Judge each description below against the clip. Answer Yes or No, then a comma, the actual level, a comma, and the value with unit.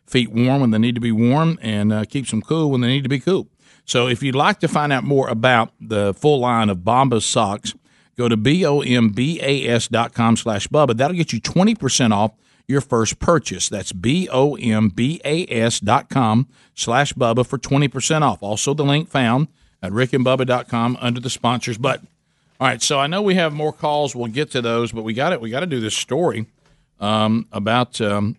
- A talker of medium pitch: No, low, 125 Hz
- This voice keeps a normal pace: No, fast, 230 wpm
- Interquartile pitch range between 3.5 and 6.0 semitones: Yes, average, 3.9 semitones